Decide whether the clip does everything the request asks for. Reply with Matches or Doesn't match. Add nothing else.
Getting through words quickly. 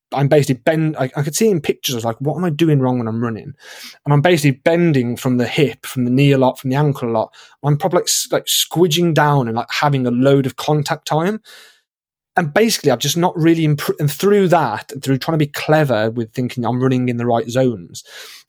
Matches